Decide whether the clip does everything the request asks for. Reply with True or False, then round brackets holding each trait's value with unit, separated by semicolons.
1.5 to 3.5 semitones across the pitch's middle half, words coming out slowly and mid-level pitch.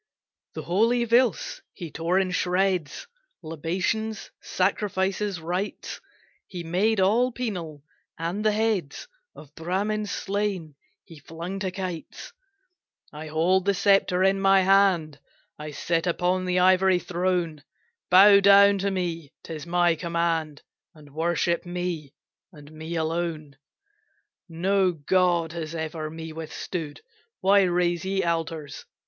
True (3.0 semitones; 125 wpm; 180 Hz)